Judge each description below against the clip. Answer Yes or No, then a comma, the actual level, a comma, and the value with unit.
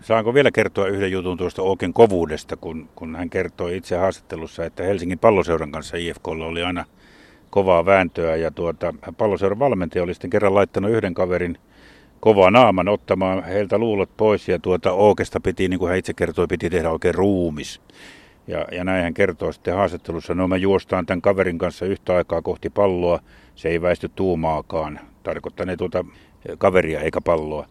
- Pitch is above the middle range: No, very low, 90 Hz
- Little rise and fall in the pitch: Yes, narrow, 2.3 semitones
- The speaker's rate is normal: No, fast, 170 wpm